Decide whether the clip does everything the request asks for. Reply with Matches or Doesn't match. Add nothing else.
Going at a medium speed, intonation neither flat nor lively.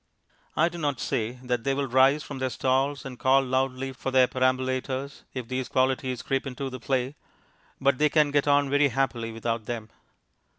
Doesn't match